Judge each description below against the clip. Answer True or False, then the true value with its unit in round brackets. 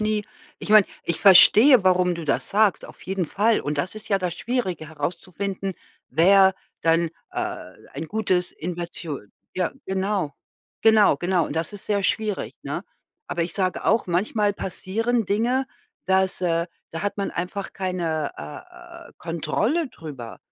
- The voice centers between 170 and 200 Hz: True (190 Hz)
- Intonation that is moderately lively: True (3.8 semitones)